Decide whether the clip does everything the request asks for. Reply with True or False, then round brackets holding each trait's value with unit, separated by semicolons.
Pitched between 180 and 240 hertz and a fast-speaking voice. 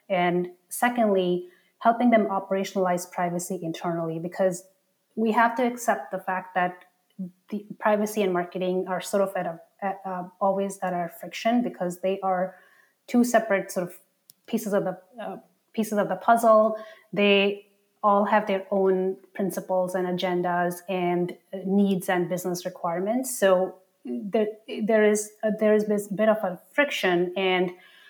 False (190 Hz; 150 wpm)